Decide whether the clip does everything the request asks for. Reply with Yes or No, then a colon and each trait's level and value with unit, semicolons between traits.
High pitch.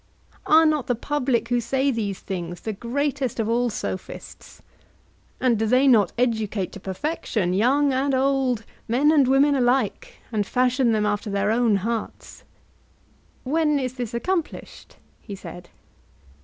Yes: high, 245 Hz